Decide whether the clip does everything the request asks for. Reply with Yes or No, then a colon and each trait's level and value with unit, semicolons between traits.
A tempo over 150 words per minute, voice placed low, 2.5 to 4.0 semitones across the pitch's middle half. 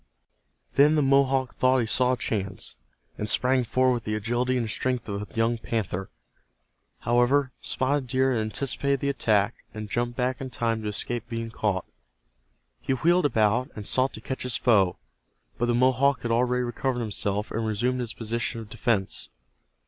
Yes: average, 175 wpm; low, 120 Hz; average, 2.9 semitones